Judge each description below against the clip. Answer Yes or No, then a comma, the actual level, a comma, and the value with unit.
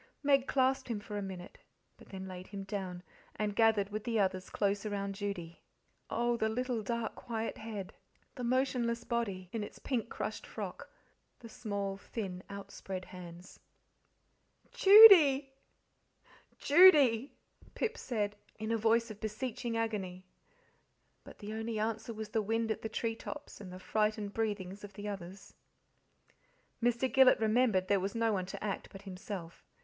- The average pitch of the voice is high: Yes, high, 215 Hz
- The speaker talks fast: No, average, 155 wpm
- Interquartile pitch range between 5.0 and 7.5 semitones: No, average, 3.0 semitones